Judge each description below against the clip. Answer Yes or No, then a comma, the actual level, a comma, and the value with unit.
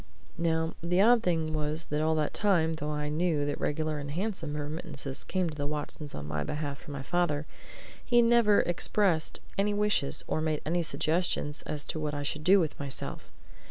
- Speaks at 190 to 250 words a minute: Yes, average, 195 wpm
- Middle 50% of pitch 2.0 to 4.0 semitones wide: Yes, average, 3.1 semitones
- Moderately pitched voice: Yes, medium, 155 Hz